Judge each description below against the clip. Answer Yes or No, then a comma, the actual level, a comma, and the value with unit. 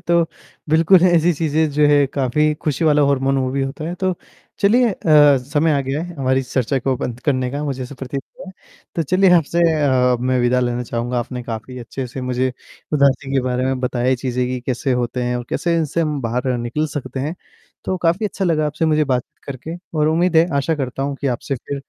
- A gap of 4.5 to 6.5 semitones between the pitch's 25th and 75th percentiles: No, average, 3.7 semitones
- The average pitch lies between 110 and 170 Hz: Yes, medium, 140 Hz